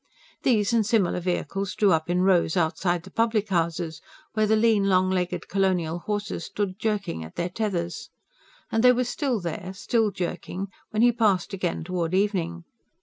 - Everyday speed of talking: Yes, average, 170 wpm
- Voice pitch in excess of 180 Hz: Yes, high, 190 Hz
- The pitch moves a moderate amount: Yes, average, 3.5 semitones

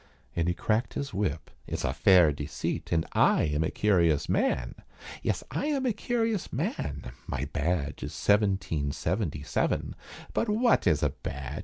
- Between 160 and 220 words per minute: Yes, average, 165 wpm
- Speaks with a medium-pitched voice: No, very low, 85 Hz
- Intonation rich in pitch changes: Yes, wide, 6.8 semitones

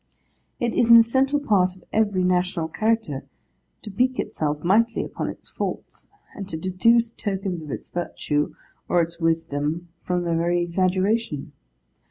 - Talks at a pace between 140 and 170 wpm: Yes, average, 150 wpm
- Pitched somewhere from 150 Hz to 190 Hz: Yes, medium, 185 Hz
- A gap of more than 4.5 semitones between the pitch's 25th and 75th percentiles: Yes, average, 4.9 semitones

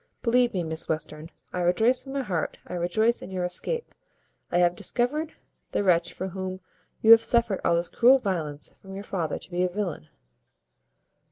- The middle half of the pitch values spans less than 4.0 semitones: No, average, 5.1 semitones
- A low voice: No, medium, 185 Hz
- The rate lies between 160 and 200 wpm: Yes, average, 185 wpm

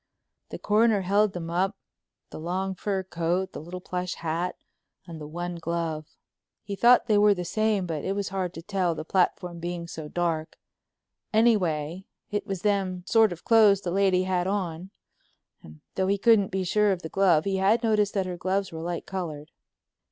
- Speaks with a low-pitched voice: No, medium, 185 Hz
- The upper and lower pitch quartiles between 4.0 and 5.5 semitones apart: No, average, 2.7 semitones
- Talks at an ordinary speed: Yes, average, 185 wpm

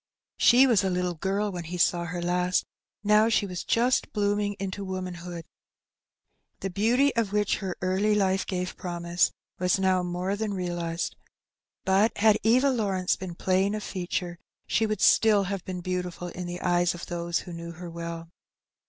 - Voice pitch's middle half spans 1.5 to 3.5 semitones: Yes, average, 2.7 semitones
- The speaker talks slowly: No, average, 170 wpm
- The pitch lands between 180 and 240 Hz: Yes, medium, 185 Hz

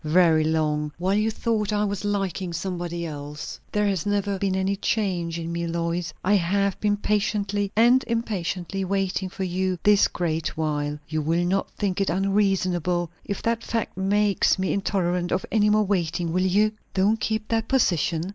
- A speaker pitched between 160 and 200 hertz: Yes, high, 190 Hz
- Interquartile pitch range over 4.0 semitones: No, average, 3.2 semitones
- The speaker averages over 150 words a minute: Yes, average, 175 wpm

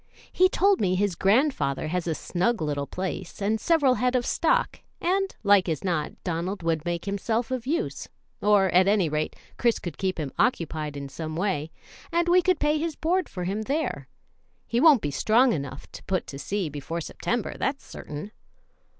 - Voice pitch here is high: Yes, high, 195 Hz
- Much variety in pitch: Yes, wide, 7.8 semitones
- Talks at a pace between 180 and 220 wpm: Yes, average, 185 wpm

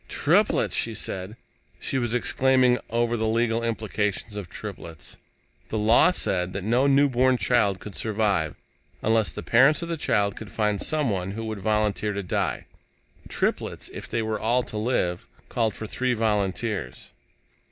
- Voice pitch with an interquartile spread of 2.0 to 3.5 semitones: Yes, average, 2.9 semitones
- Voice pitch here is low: Yes, low, 110 Hz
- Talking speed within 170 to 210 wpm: No, average, 155 wpm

